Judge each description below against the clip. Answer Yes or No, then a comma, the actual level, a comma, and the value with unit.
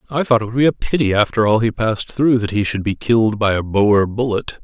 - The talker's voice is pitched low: Yes, low, 110 Hz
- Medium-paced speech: No, fast, 270 wpm